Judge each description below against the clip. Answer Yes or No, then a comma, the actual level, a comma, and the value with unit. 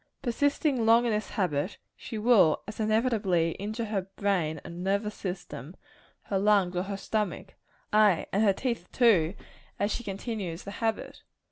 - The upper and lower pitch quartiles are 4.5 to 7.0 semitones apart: No, average, 3.5 semitones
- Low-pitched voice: No, high, 205 Hz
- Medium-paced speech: Yes, average, 155 wpm